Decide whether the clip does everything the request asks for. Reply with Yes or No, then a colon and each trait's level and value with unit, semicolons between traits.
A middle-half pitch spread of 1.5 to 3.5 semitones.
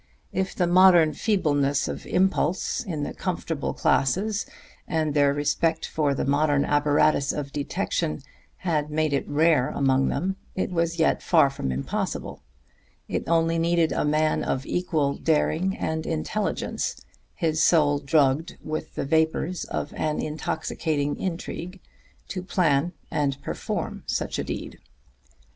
Yes: average, 2.7 semitones